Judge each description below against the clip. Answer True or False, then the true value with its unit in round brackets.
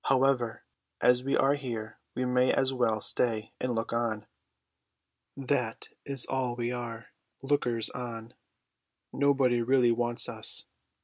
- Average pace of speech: False (130 wpm)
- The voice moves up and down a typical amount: False (2.2 semitones)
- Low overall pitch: True (125 Hz)